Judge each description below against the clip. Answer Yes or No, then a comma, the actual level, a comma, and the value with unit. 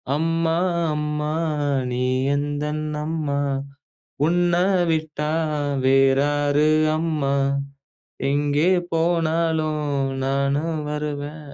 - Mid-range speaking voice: Yes, medium, 150 Hz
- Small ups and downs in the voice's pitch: Yes, narrow, 2.0 semitones